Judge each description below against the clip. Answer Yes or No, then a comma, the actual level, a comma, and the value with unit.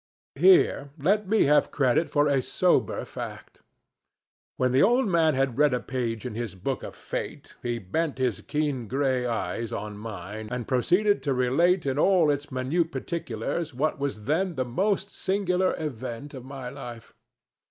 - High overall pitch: No, low, 135 Hz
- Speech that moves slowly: No, average, 165 wpm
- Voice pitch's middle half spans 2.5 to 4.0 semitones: No, average, 5.2 semitones